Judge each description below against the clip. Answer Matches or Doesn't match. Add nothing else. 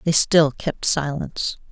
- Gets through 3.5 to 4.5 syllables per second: Matches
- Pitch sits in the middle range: Matches